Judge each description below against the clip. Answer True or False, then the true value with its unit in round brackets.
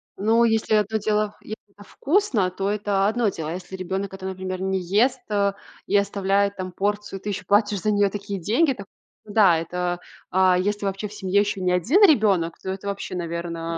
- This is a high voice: True (200 Hz)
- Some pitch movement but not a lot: False (2.0 semitones)